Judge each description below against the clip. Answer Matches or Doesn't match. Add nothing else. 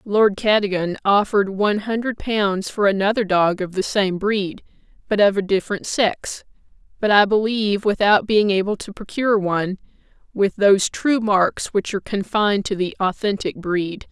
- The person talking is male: Doesn't match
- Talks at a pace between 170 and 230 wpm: Doesn't match